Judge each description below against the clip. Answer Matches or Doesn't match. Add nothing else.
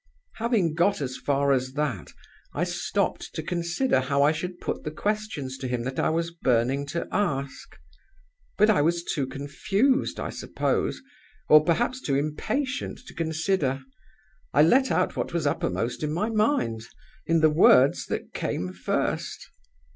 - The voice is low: Doesn't match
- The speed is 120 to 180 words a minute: Matches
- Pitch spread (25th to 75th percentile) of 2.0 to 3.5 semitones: Doesn't match